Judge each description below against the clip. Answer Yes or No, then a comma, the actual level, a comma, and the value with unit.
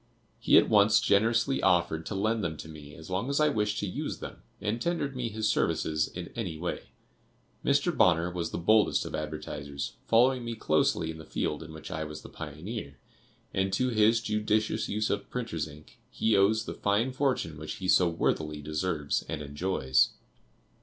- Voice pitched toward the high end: No, very low, 95 Hz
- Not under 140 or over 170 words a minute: No, average, 185 wpm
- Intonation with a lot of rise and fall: Yes, wide, 5.9 semitones